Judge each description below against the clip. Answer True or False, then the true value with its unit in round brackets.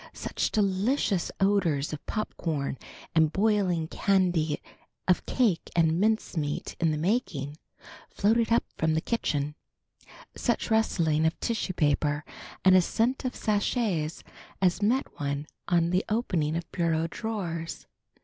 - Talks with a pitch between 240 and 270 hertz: False (175 Hz)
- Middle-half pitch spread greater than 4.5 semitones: True (5.2 semitones)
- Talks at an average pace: False (125 wpm)